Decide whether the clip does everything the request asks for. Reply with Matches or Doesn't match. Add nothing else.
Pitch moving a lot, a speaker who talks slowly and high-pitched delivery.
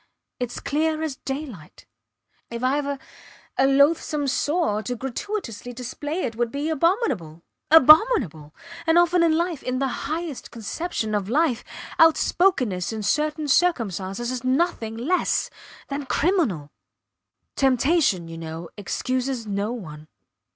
Matches